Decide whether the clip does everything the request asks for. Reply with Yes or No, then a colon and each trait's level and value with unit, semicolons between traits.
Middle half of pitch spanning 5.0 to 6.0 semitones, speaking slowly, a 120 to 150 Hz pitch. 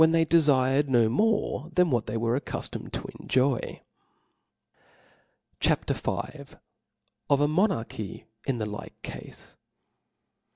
Yes: wide, 5.5 semitones; slow, 120 wpm; low, 135 Hz